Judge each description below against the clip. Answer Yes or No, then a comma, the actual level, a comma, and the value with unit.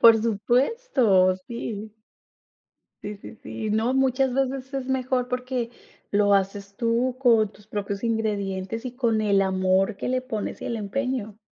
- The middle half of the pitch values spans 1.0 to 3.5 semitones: No, average, 3.9 semitones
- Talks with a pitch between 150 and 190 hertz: No, high, 225 Hz